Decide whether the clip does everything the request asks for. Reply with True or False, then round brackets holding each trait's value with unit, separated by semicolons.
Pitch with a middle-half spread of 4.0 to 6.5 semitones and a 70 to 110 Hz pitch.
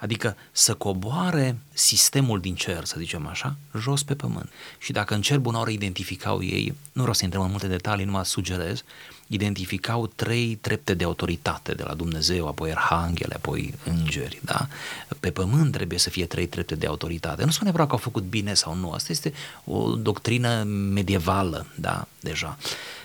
True (4.7 semitones; 100 Hz)